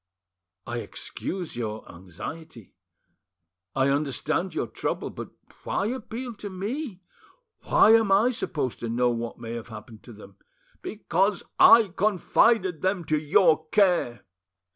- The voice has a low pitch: No, medium, 160 Hz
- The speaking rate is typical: No, slow, 130 wpm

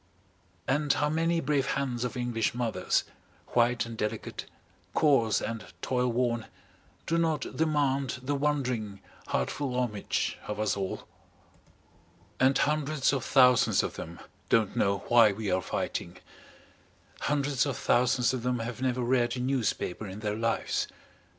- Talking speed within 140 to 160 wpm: Yes, average, 145 wpm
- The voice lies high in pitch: No, low, 125 Hz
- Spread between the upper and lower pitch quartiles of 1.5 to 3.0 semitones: No, average, 3.5 semitones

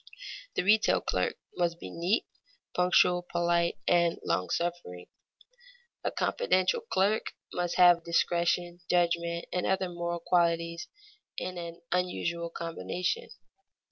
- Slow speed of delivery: Yes, slow, 110 wpm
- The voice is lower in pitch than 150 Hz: No, medium, 175 Hz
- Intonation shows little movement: Yes, narrow, 1.1 semitones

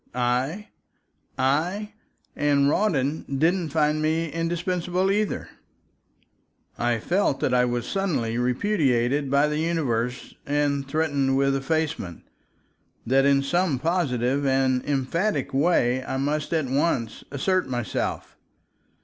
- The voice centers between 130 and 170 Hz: Yes, medium, 140 Hz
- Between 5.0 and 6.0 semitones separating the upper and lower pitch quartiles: No, average, 4.2 semitones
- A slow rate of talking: Yes, slow, 110 wpm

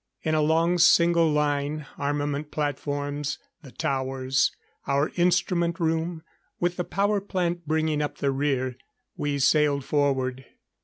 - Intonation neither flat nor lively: Yes, average, 3.0 semitones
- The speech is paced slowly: Yes, slow, 125 wpm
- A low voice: No, medium, 150 Hz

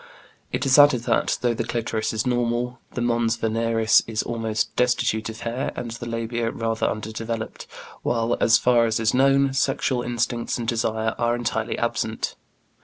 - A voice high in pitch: No, low, 115 Hz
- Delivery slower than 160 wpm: No, average, 165 wpm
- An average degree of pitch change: No, narrow, 1.3 semitones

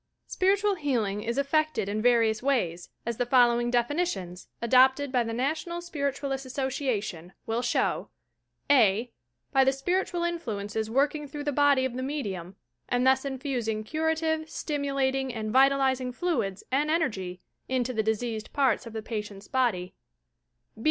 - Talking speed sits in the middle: Yes, average, 150 wpm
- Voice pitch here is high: Yes, very high, 260 Hz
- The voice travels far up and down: No, average, 4.4 semitones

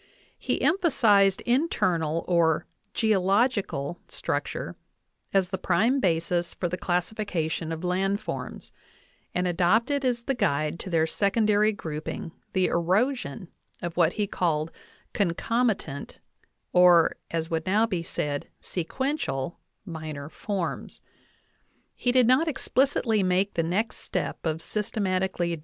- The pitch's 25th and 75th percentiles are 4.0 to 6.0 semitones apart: Yes, average, 4.7 semitones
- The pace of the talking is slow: Yes, slow, 125 wpm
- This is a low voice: No, medium, 185 Hz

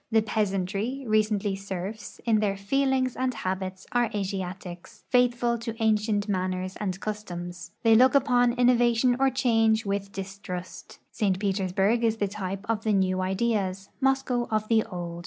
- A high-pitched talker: Yes, high, 210 Hz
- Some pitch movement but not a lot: Yes, average, 3.7 semitones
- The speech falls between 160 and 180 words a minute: No, average, 150 wpm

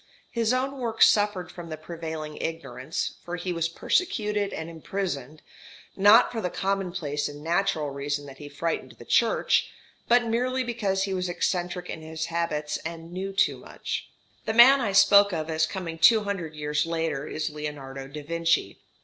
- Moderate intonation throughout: Yes, average, 4.5 semitones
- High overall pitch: No, medium, 170 Hz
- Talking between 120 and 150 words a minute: No, average, 170 wpm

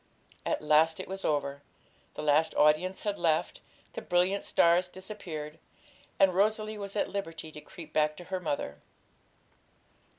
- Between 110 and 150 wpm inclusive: Yes, average, 145 wpm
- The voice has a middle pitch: Yes, medium, 170 Hz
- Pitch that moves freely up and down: No, average, 4.1 semitones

